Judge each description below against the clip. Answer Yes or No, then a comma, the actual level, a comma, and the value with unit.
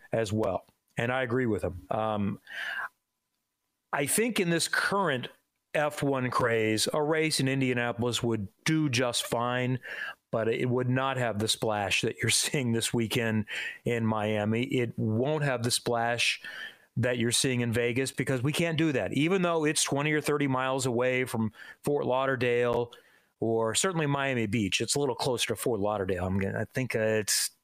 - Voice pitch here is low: Yes, low, 125 Hz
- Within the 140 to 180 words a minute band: Yes, average, 175 wpm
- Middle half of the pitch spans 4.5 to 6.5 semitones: No, average, 3.7 semitones